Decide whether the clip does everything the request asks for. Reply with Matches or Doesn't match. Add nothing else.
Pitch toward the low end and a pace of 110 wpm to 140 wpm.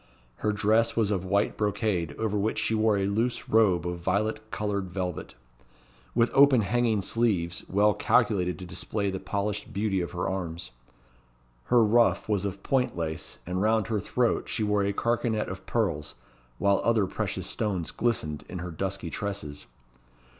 Doesn't match